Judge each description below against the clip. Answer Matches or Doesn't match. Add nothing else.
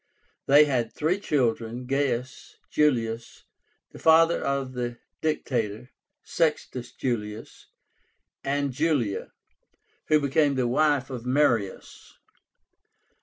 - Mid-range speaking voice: Doesn't match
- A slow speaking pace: Matches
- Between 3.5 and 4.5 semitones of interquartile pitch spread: Matches